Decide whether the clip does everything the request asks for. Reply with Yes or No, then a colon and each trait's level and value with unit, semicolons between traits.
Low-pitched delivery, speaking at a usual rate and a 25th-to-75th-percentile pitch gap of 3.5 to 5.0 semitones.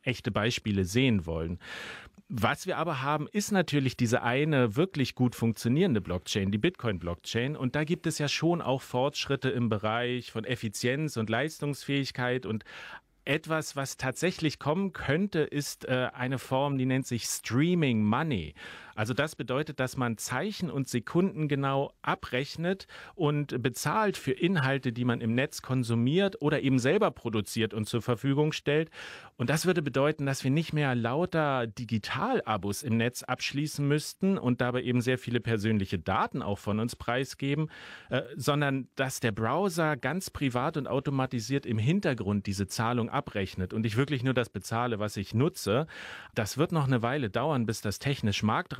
Yes: low, 130 Hz; average, 160 wpm; average, 4.2 semitones